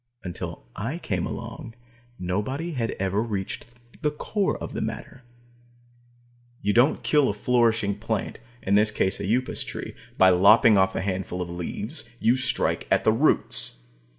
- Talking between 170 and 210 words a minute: No, average, 155 wpm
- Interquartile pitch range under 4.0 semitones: No, average, 4.6 semitones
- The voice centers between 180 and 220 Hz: No, low, 105 Hz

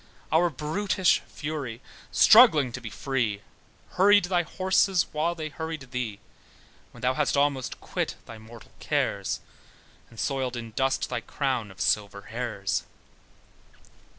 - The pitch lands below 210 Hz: Yes, low, 135 Hz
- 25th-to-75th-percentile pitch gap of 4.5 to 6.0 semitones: Yes, wide, 5.6 semitones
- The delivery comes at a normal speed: No, slow, 130 wpm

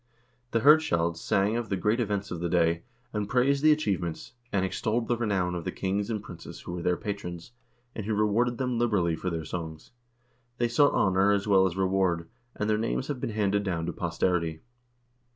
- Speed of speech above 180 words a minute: Yes, average, 200 wpm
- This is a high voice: No, low, 100 Hz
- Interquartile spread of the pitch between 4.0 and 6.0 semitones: Yes, average, 4.5 semitones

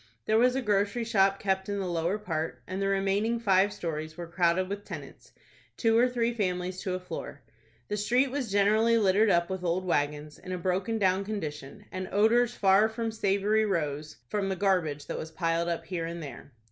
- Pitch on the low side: No, high, 195 Hz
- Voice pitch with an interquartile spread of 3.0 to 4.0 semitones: Yes, average, 3.7 semitones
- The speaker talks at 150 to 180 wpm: No, average, 200 wpm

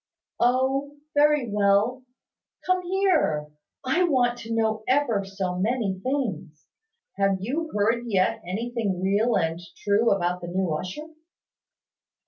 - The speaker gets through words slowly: Yes, slow, 120 wpm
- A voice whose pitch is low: No, high, 220 Hz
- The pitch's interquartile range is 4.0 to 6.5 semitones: Yes, wide, 5.5 semitones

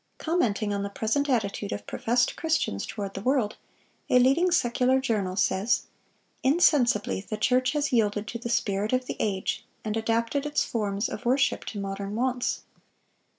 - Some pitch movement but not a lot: Yes, average, 4.1 semitones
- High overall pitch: Yes, high, 230 Hz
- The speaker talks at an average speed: Yes, average, 160 wpm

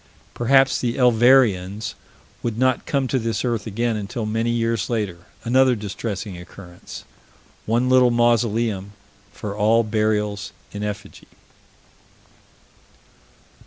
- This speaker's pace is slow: Yes, slow, 110 wpm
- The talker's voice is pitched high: No, low, 115 Hz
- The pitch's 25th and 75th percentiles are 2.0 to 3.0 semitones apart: Yes, narrow, 2.6 semitones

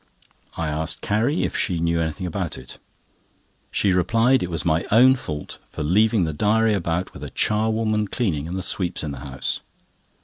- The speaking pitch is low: Yes, very low, 90 Hz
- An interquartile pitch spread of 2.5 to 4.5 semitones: No, average, 5.3 semitones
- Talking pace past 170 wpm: Yes, average, 180 wpm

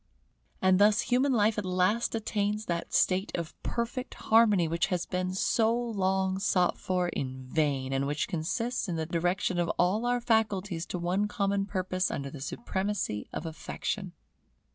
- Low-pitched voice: No, high, 190 Hz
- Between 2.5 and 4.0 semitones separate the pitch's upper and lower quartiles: Yes, average, 3.6 semitones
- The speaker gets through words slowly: No, average, 165 wpm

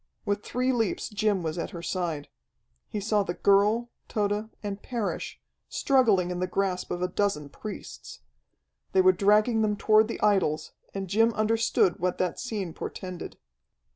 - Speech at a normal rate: Yes, average, 160 wpm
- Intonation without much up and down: No, average, 3.1 semitones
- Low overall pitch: No, high, 200 Hz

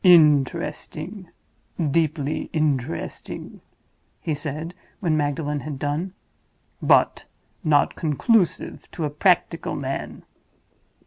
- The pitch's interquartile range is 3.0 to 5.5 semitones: No, narrow, 2.5 semitones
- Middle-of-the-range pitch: Yes, medium, 155 Hz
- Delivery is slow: Yes, slow, 85 wpm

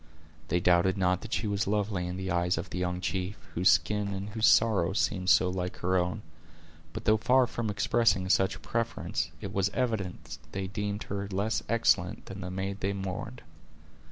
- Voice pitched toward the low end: Yes, very low, 95 Hz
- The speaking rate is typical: Yes, average, 190 wpm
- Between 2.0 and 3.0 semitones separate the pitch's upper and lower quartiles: Yes, narrow, 2.6 semitones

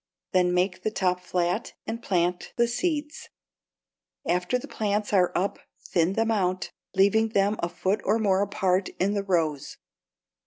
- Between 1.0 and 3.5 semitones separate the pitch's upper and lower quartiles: Yes, average, 3.1 semitones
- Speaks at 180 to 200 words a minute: No, average, 155 wpm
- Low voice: No, high, 195 Hz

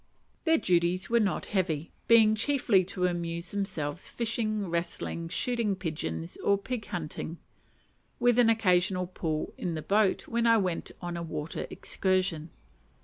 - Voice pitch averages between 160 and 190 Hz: Yes, medium, 185 Hz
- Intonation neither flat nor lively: Yes, average, 4.3 semitones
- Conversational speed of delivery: Yes, average, 145 wpm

